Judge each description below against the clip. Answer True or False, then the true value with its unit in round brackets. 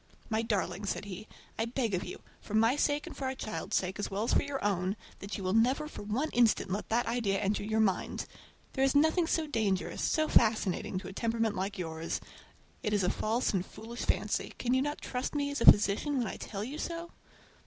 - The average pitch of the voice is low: False (220 Hz)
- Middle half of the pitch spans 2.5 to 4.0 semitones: False (4.9 semitones)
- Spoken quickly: True (230 wpm)